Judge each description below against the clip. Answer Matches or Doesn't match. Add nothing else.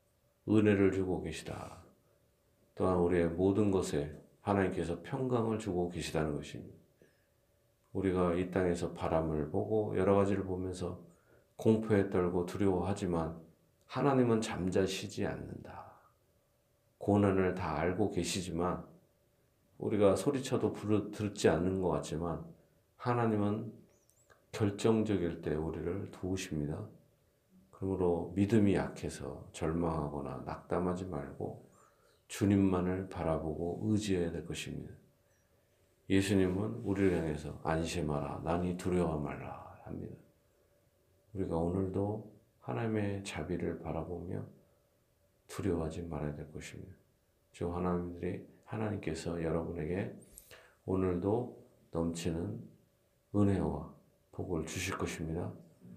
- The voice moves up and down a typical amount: Matches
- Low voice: Matches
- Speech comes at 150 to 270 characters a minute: Matches